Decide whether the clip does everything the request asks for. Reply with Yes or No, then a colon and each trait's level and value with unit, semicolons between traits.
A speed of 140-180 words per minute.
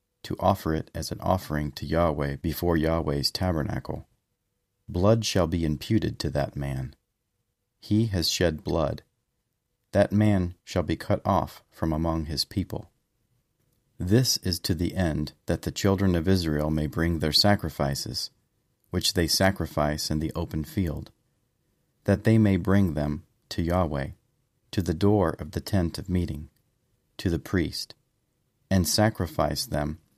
Yes: average, 145 wpm